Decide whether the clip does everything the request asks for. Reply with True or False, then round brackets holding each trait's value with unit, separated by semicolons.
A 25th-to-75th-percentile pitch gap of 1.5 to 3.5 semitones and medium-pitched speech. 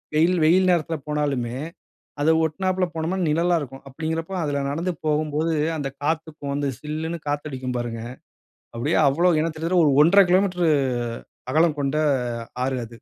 True (2.8 semitones; 155 Hz)